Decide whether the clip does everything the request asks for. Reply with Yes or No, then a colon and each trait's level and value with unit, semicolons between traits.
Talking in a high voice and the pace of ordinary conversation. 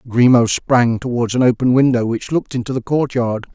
No: low, 125 Hz; average, 185 wpm